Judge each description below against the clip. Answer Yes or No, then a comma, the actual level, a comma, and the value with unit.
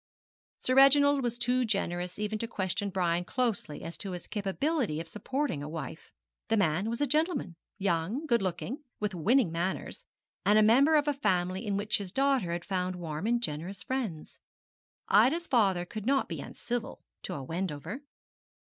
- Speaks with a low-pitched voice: No, high, 205 Hz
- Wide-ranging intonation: Yes, wide, 6.1 semitones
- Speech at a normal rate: Yes, average, 170 wpm